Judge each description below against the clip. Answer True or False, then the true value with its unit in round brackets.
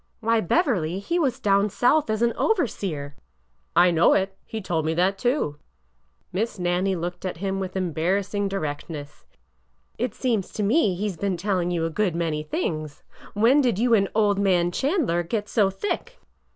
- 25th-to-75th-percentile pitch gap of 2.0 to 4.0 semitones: False (4.4 semitones)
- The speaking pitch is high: True (195 Hz)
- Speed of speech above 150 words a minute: True (190 wpm)